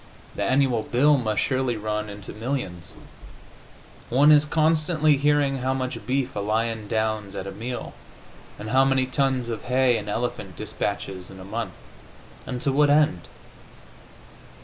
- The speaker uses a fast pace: No, average, 150 wpm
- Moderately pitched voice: No, low, 125 Hz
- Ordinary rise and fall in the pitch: Yes, average, 4.3 semitones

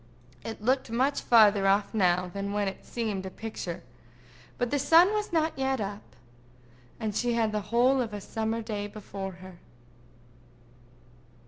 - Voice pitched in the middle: No, high, 220 Hz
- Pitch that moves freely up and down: No, average, 3.6 semitones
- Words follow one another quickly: No, average, 155 wpm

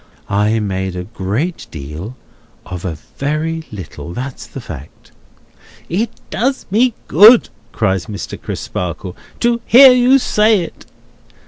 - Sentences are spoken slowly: Yes, slow, 125 wpm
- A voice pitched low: Yes, low, 125 Hz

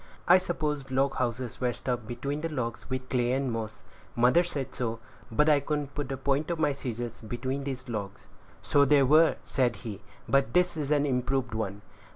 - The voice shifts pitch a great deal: No, average, 3.3 semitones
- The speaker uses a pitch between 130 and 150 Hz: Yes, low, 135 Hz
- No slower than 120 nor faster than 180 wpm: No, average, 195 wpm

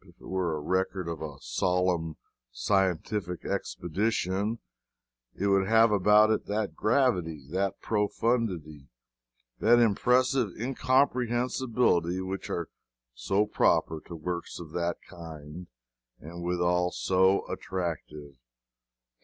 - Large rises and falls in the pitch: No, average, 4.1 semitones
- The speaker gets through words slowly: Yes, slow, 110 wpm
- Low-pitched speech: Yes, very low, 95 Hz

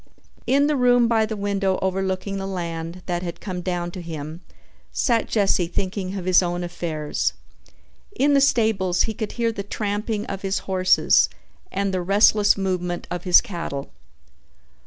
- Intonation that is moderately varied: Yes, average, 3.0 semitones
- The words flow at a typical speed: Yes, average, 160 wpm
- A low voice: No, high, 190 Hz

